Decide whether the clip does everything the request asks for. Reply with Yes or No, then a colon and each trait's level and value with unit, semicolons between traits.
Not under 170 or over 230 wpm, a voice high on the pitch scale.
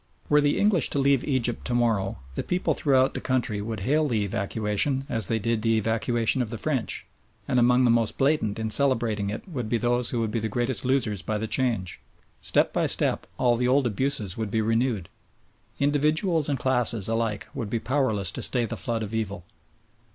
No: fast, 205 wpm; low, 120 Hz